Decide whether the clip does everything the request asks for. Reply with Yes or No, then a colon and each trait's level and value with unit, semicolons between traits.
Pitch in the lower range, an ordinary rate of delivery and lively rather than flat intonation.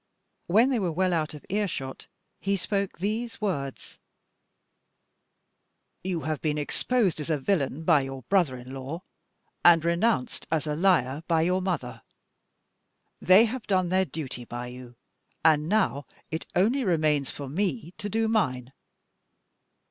No: medium, 165 Hz; average, 150 wpm; wide, 5.8 semitones